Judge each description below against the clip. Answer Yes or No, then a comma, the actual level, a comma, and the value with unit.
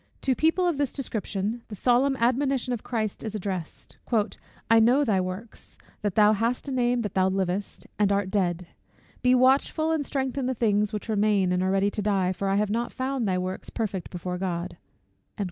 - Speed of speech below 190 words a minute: No, average, 195 wpm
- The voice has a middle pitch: No, high, 215 Hz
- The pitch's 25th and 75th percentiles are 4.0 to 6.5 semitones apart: Yes, average, 4.6 semitones